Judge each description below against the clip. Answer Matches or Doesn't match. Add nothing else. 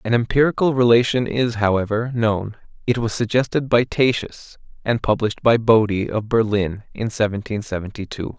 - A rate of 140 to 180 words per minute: Matches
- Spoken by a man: Matches